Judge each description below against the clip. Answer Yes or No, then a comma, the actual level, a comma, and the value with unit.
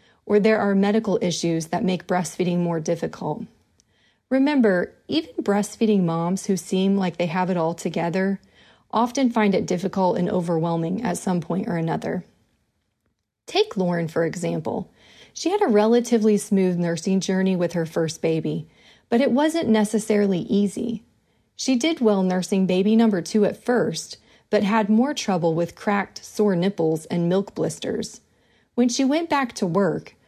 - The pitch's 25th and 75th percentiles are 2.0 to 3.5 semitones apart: No, average, 4.0 semitones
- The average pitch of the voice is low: No, high, 195 Hz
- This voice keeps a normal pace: Yes, average, 155 wpm